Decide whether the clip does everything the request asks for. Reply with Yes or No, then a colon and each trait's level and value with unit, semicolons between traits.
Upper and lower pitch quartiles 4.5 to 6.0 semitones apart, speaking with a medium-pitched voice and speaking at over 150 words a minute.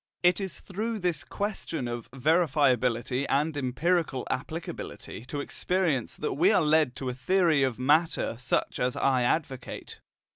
No: average, 5.2 semitones; medium, 145 Hz; average, 145 wpm